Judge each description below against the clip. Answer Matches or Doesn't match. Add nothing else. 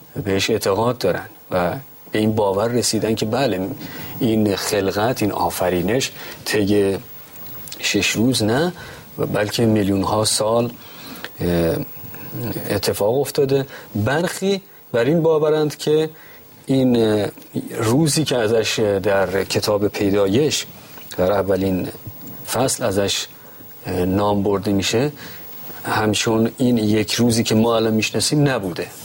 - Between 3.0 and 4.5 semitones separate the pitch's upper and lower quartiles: Doesn't match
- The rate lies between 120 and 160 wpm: Doesn't match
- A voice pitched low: Matches